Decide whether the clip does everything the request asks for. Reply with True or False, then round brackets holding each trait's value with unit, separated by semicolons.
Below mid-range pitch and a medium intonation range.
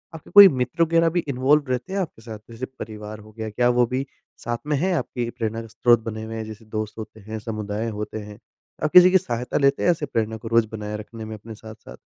True (115 Hz; 4.0 semitones)